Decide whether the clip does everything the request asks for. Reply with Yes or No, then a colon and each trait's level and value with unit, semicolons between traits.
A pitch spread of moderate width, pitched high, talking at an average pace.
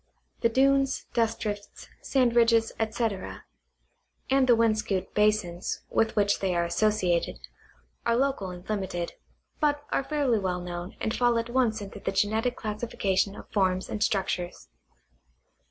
Yes: average, 3.6 semitones; high, 215 Hz; average, 145 wpm